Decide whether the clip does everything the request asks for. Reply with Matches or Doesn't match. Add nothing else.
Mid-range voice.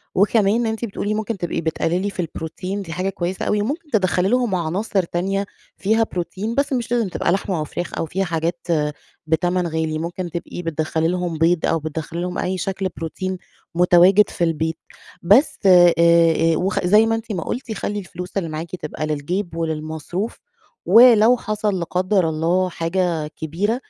Matches